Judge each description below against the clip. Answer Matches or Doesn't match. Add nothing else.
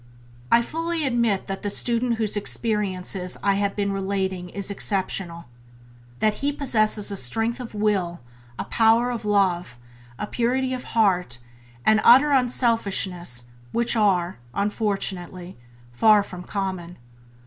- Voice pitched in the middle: Doesn't match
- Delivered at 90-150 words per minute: Matches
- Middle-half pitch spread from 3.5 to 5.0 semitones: Matches